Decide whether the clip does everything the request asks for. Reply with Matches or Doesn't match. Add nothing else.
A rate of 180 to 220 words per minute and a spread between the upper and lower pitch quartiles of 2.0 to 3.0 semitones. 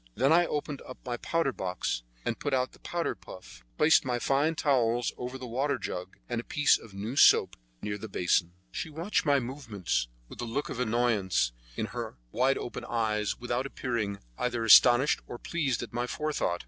Doesn't match